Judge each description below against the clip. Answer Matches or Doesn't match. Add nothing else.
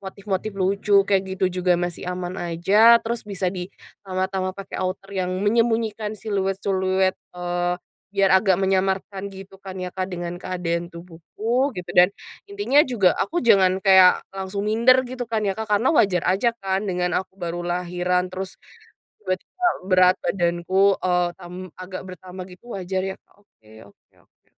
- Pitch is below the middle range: Doesn't match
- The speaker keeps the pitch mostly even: Matches